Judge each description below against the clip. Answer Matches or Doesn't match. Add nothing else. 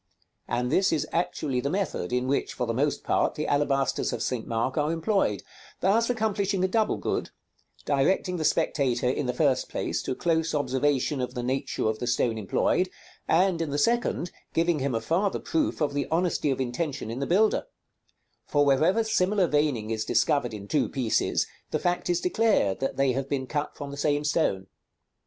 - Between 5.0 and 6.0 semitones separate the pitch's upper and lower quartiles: Matches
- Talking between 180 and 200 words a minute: Matches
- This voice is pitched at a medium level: Matches